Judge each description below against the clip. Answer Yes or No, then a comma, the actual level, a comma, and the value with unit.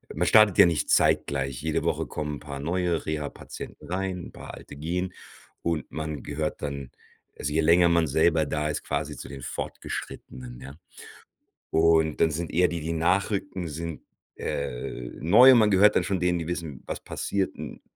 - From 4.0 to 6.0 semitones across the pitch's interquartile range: No, average, 3.2 semitones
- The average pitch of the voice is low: Yes, very low, 80 Hz